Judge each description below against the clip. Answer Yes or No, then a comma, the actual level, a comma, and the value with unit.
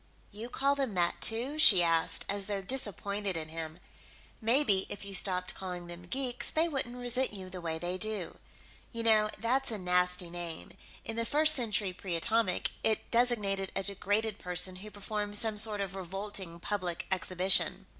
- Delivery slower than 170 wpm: No, average, 175 wpm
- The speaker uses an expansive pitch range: No, average, 4.1 semitones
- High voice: Yes, high, 200 Hz